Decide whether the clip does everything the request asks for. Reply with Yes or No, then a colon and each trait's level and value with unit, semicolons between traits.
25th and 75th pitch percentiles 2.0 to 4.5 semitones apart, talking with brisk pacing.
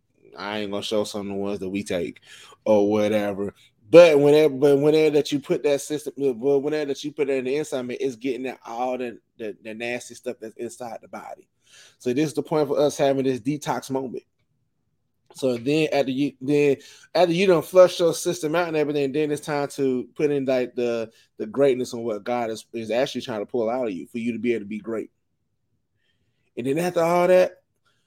Yes: average, 4.0 semitones; fast, 225 wpm